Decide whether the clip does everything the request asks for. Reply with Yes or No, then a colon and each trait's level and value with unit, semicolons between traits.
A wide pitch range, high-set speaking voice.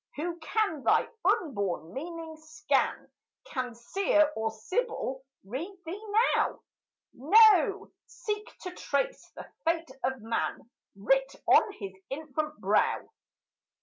Yes: wide, 6.8 semitones; very high, 310 Hz